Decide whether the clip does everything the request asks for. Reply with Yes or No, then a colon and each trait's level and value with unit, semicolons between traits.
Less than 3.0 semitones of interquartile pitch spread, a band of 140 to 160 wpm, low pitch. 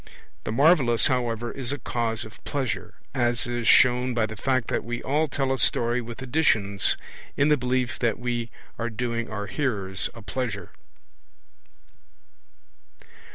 Yes: narrow, 2.4 semitones; average, 150 wpm; low, 120 Hz